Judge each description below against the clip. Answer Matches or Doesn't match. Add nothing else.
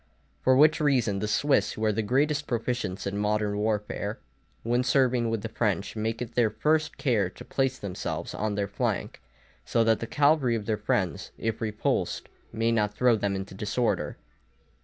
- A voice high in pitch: Doesn't match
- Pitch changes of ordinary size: Matches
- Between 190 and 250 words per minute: Doesn't match